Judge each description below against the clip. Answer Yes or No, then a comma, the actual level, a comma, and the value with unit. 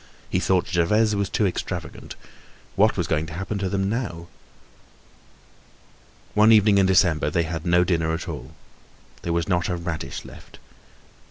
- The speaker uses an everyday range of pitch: Yes, average, 3.1 semitones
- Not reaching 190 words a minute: Yes, average, 160 wpm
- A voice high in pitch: No, very low, 90 Hz